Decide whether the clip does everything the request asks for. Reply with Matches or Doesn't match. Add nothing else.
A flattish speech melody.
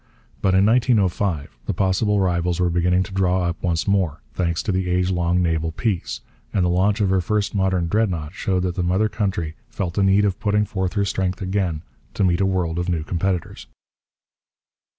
Matches